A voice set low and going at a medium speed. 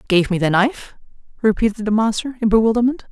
No: high, 220 Hz; average, 175 wpm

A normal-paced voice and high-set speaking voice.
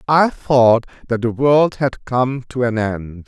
No: average, 185 wpm; low, 125 Hz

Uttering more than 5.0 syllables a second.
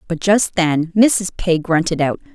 No: 4.1 syllables/s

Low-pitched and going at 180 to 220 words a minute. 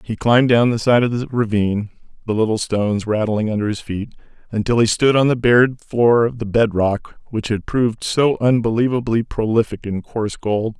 Yes: low, 115 Hz; average, 195 wpm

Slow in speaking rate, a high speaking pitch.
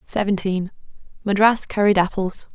Yes: slow, 70 wpm; high, 195 Hz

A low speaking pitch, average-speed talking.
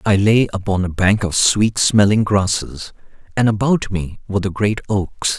Yes: low, 100 Hz; average, 180 wpm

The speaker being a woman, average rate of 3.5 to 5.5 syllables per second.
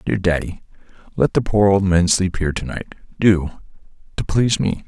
No: male; 5.2 syllables/s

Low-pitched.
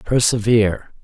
Yes: low, 110 Hz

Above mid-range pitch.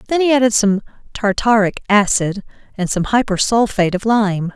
Yes: high, 210 Hz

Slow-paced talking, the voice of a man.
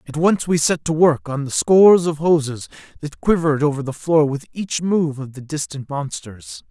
No: fast, 205 wpm; male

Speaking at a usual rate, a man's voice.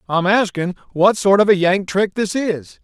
No: fast, 210 wpm; male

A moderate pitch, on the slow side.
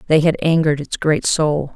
No: medium, 155 Hz; fast, 205 wpm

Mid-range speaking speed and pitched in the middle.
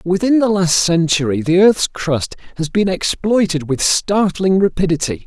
Yes: average, 150 wpm; medium, 180 Hz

